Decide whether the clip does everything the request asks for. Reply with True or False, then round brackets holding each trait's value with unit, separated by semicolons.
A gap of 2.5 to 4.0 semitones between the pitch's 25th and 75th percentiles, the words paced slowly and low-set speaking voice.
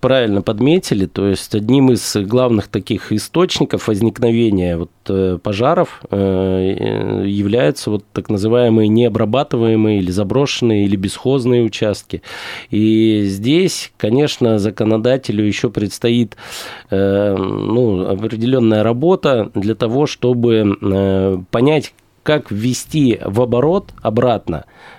True (3.6 semitones; 95 wpm; 110 Hz)